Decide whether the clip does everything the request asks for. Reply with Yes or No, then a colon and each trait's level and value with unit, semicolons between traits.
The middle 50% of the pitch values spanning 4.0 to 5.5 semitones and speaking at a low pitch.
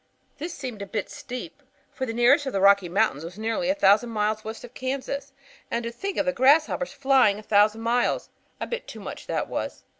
No: average, 4.4 semitones; high, 235 Hz